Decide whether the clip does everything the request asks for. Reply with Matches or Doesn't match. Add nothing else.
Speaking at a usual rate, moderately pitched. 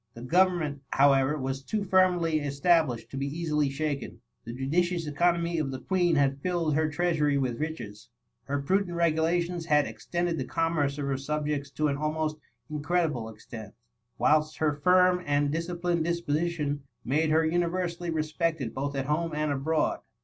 Matches